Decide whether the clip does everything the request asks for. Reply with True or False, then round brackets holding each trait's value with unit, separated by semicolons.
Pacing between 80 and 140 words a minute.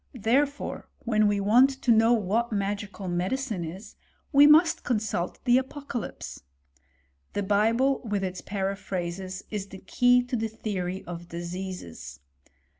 True (135 wpm)